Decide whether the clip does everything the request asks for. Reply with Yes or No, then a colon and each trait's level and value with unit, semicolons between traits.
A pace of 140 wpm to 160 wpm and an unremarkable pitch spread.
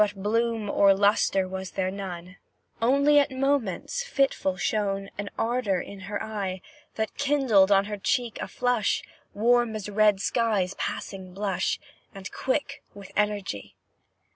Yes: average, 145 wpm; average, 3.5 semitones